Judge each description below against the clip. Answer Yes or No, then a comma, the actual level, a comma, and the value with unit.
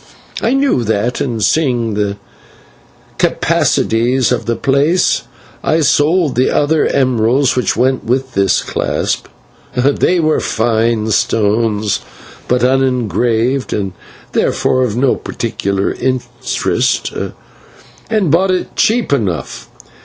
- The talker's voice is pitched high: No, low, 125 Hz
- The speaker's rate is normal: No, slow, 110 wpm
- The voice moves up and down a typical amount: Yes, average, 4.0 semitones